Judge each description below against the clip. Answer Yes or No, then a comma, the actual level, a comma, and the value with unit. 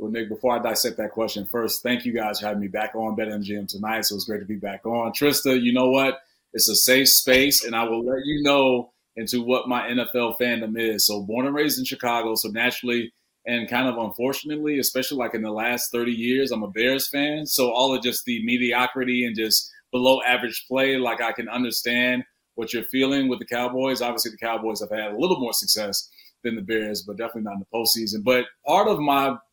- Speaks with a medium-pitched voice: No, low, 120 Hz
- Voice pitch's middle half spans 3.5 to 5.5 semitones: No, narrow, 2.5 semitones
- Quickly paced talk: Yes, fast, 225 wpm